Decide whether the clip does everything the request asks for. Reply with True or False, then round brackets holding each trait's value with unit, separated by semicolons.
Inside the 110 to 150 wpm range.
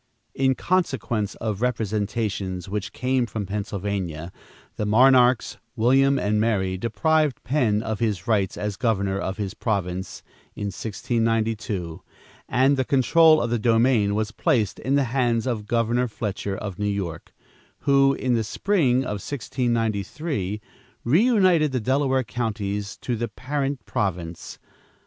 True (135 wpm)